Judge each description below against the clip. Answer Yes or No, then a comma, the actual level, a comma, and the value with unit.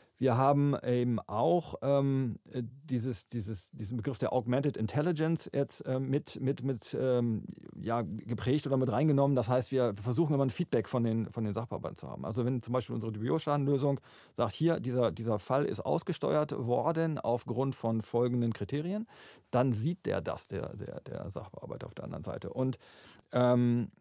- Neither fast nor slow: Yes, average, 170 wpm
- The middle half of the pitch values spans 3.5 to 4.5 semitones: No, average, 2.9 semitones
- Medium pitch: No, low, 130 Hz